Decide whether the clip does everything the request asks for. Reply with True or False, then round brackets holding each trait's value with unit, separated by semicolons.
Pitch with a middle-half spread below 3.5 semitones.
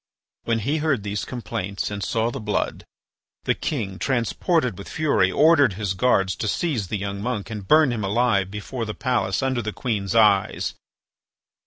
False (4.2 semitones)